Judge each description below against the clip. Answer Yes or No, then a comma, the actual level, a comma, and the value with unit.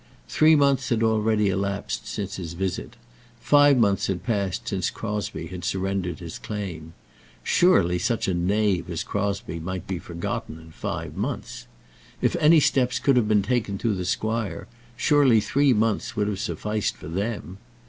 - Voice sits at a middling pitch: No, low, 100 Hz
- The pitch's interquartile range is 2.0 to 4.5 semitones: Yes, average, 3.7 semitones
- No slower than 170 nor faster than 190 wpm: No, average, 160 wpm